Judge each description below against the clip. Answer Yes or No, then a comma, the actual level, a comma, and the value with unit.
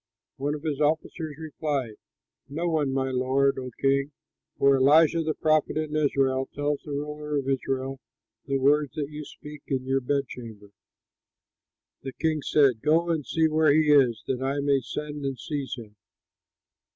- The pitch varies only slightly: Yes, narrow, 2.2 semitones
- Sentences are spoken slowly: No, average, 165 wpm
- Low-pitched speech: No, medium, 145 Hz